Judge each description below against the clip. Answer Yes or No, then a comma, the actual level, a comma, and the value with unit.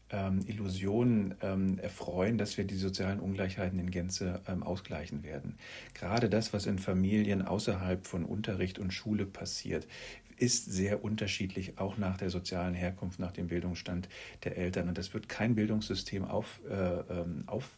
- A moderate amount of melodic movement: No, narrow, 2.3 semitones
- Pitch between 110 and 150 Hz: No, very low, 95 Hz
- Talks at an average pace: Yes, average, 145 wpm